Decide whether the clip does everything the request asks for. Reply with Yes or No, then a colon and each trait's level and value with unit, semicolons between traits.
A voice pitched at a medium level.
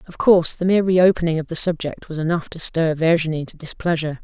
Yes: medium, 165 Hz